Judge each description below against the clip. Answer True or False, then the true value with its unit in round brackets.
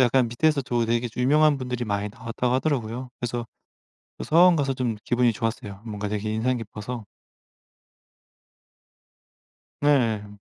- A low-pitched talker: True (120 Hz)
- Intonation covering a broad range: False (2.7 semitones)